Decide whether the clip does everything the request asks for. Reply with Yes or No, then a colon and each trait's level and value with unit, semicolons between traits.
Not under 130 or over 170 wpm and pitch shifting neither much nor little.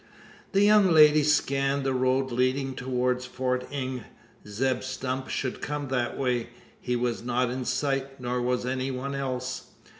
No: average, 155 wpm; narrow, 1.4 semitones